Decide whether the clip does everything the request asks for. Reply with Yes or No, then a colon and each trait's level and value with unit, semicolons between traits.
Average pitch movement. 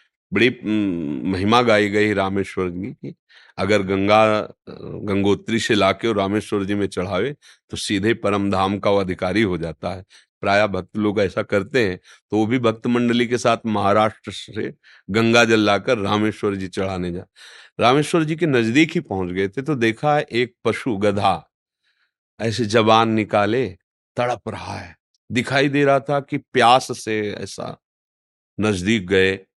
Yes: average, 3.0 semitones